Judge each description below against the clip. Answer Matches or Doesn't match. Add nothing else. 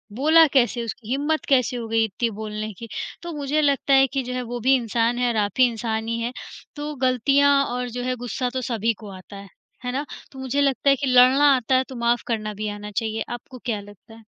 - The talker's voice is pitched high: Matches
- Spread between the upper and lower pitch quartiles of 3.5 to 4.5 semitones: Doesn't match